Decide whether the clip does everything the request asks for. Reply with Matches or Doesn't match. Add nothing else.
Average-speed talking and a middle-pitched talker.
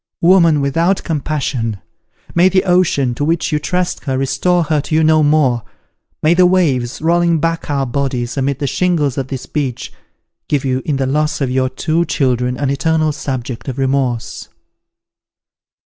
Matches